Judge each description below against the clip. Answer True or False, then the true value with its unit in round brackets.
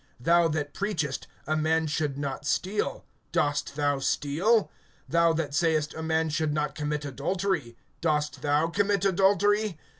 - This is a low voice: False (155 Hz)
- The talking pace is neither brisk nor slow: True (145 wpm)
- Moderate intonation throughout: True (3.4 semitones)